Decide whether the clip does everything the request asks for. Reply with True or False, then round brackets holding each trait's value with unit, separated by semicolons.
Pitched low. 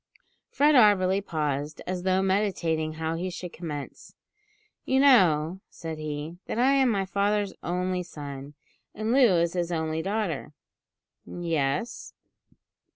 False (180 Hz)